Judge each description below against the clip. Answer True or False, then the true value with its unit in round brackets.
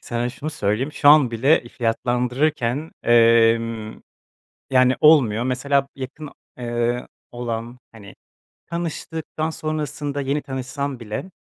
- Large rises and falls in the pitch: False (3.8 semitones)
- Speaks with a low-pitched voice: True (125 Hz)